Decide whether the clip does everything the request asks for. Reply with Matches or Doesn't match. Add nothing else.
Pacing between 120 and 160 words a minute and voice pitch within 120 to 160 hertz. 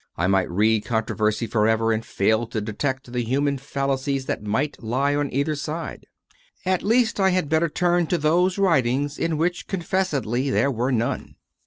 Doesn't match